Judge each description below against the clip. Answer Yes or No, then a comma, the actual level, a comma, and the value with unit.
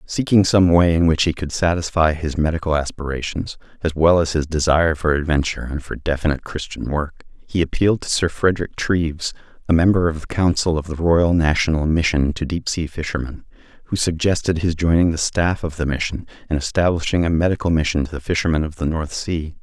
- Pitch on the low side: Yes, very low, 80 Hz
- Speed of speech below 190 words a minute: No, average, 195 wpm